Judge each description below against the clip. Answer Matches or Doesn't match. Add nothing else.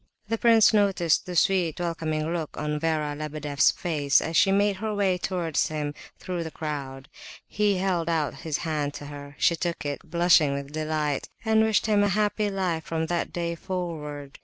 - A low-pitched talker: Doesn't match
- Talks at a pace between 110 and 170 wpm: Doesn't match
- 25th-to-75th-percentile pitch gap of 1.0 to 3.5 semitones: Doesn't match